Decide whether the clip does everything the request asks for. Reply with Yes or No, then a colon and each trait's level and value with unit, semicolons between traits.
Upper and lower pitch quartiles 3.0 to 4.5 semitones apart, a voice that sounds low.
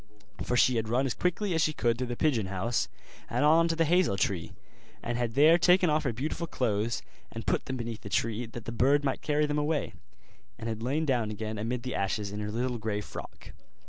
No: average, 5.2 semitones; low, 120 Hz